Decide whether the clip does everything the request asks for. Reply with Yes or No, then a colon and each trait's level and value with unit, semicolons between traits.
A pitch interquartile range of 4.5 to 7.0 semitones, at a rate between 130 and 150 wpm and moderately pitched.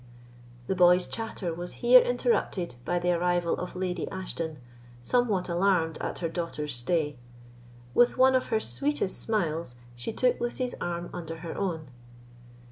Yes: average, 4.9 semitones; average, 145 wpm; medium, 180 Hz